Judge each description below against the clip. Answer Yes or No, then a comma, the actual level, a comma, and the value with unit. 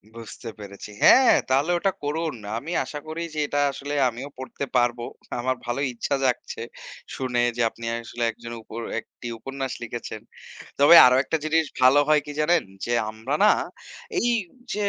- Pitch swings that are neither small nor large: Yes, average, 4.0 semitones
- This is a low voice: Yes, low, 130 Hz